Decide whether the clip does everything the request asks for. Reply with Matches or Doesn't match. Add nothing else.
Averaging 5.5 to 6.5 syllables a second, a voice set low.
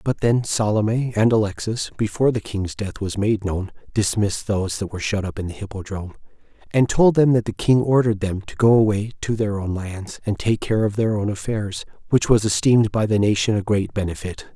Matches